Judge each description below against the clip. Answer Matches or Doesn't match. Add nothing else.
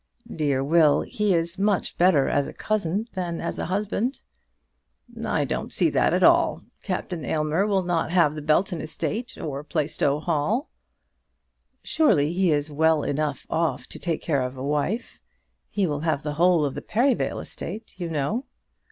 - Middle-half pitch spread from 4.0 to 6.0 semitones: Matches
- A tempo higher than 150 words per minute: Matches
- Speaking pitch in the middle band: Matches